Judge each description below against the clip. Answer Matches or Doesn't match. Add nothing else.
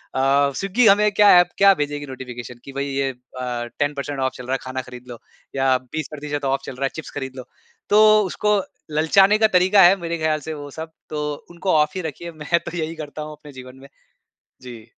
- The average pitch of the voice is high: Doesn't match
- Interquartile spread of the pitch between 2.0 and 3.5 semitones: Doesn't match